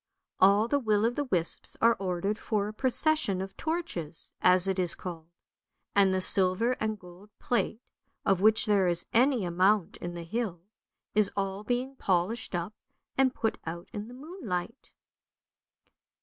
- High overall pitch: Yes, high, 200 Hz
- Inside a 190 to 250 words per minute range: No, average, 160 wpm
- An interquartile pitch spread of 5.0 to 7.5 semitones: No, average, 4.4 semitones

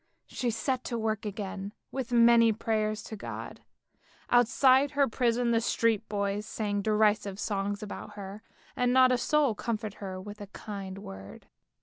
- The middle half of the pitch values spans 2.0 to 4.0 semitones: Yes, average, 2.7 semitones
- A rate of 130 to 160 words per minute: Yes, average, 155 wpm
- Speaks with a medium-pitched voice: No, high, 215 Hz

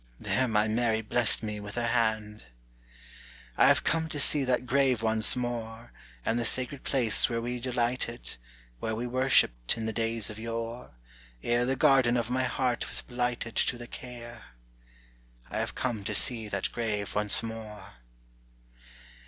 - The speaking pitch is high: No, low, 115 Hz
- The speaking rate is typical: Yes, average, 160 wpm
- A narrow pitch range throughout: Yes, narrow, 2.0 semitones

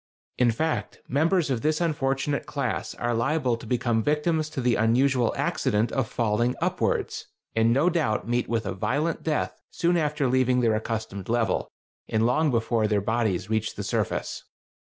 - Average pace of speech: Yes, average, 165 wpm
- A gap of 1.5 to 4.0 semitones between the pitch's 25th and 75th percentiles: No, average, 4.8 semitones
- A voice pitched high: No, low, 125 Hz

